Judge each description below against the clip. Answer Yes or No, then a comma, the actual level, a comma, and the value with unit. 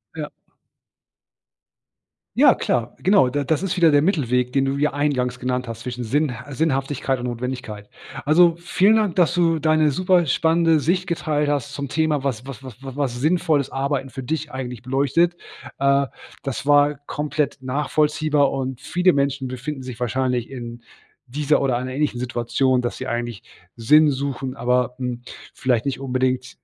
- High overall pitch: No, low, 135 Hz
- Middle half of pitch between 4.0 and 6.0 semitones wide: No, average, 3.2 semitones